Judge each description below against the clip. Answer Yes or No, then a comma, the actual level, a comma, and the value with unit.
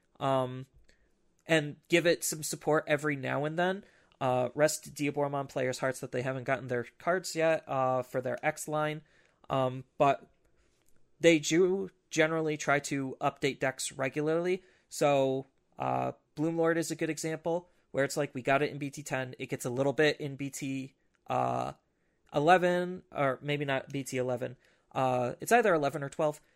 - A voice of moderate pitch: Yes, medium, 145 Hz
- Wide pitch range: No, average, 3.3 semitones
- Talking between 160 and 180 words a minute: Yes, average, 165 wpm